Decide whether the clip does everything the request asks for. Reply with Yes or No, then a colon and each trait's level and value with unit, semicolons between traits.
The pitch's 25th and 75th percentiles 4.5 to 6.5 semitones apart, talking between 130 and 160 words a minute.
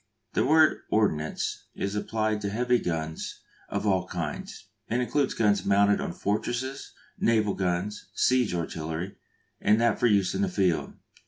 No: average, 4.1 semitones; average, 150 wpm